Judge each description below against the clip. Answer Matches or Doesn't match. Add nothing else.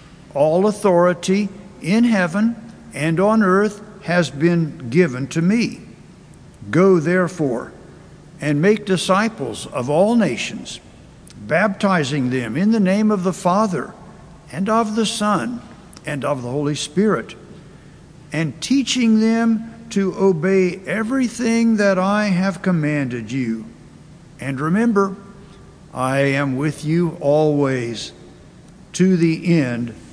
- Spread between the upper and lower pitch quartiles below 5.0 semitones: Doesn't match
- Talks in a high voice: Doesn't match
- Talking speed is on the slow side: Matches